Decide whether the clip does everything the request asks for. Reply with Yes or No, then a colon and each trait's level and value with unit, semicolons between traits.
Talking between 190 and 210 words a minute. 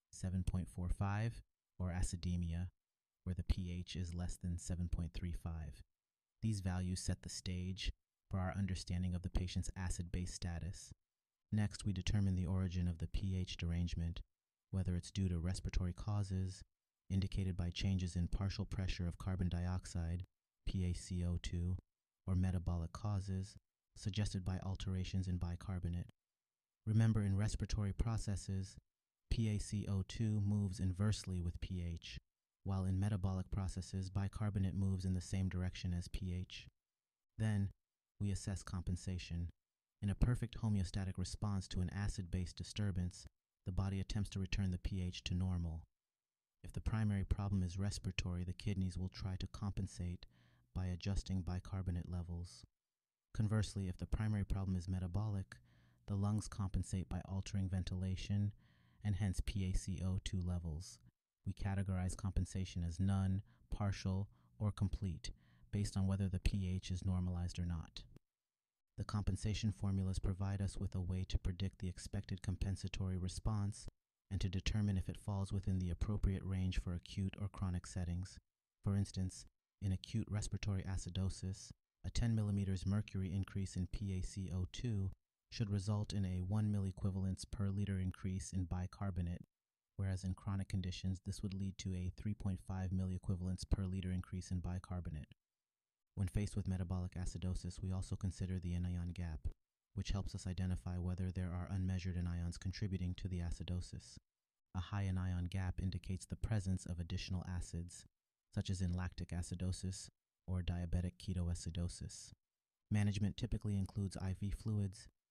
No: average, 140 wpm